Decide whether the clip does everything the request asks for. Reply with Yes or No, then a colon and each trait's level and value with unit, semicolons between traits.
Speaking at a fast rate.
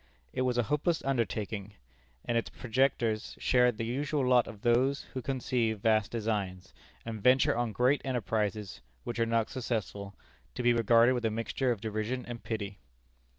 No: average, 165 wpm